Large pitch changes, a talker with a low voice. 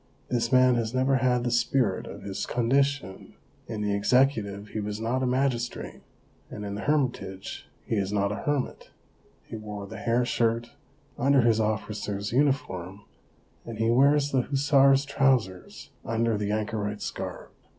No: average, 4.1 semitones; low, 115 Hz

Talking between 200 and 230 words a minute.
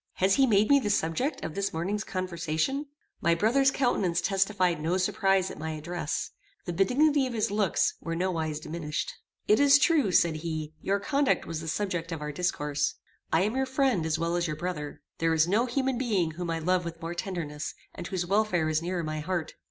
Yes: fast, 205 wpm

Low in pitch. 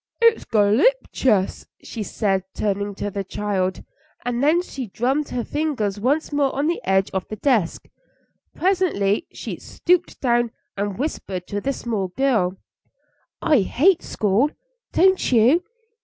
No: high, 235 Hz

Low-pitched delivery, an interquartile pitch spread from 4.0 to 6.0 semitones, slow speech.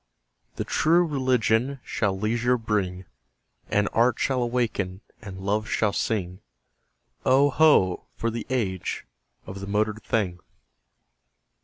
Yes: low, 110 Hz; average, 4.3 semitones; slow, 120 wpm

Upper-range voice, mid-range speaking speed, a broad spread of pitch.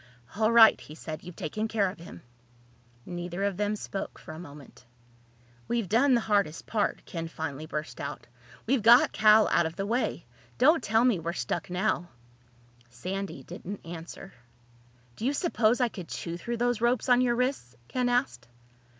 Yes: high, 200 Hz; average, 175 wpm; wide, 6.0 semitones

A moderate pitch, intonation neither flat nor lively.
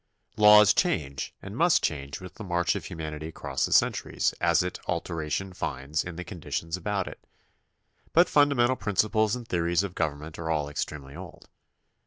No: very low, 85 Hz; average, 4.9 semitones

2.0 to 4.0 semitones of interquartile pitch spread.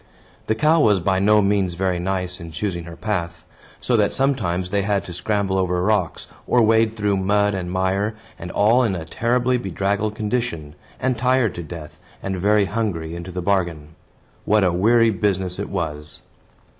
Yes: average, 3.3 semitones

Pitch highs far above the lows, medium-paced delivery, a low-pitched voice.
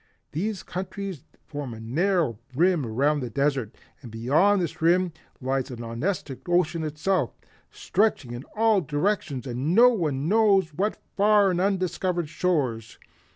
No: wide, 6.4 semitones; average, 145 wpm; medium, 165 Hz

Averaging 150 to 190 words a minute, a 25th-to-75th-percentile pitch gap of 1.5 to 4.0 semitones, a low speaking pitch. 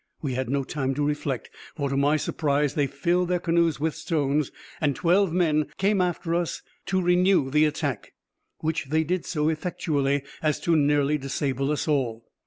No: average, 185 wpm; average, 3.3 semitones; medium, 150 Hz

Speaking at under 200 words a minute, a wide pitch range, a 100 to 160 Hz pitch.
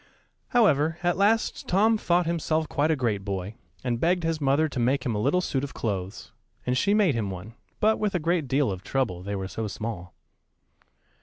No: fast, 205 wpm; wide, 8.2 semitones; medium, 140 Hz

